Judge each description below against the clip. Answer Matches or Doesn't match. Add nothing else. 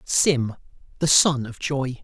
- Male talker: Matches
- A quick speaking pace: Doesn't match